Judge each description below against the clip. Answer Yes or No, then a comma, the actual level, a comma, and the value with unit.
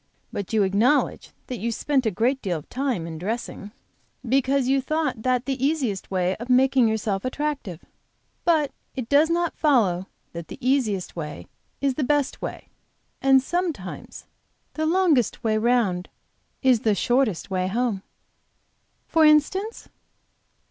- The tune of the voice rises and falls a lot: Yes, wide, 5.8 semitones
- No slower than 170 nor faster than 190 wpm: No, average, 145 wpm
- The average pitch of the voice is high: Yes, very high, 250 Hz